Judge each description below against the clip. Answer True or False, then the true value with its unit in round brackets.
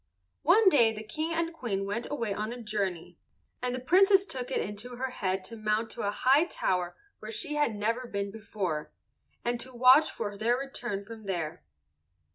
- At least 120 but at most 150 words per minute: False (190 wpm)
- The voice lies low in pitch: False (230 Hz)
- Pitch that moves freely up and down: False (4.3 semitones)